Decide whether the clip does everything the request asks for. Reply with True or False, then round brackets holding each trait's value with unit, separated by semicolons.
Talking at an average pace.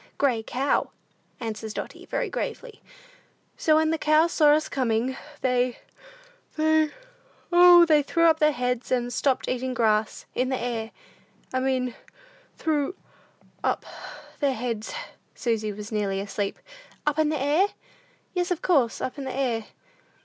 True (145 wpm)